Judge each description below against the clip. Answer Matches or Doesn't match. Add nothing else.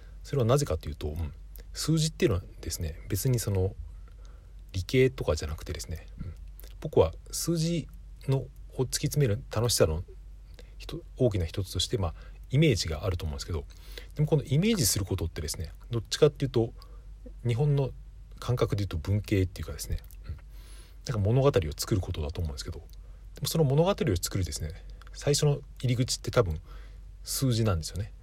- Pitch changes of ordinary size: Doesn't match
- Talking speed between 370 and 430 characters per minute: Doesn't match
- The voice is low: Matches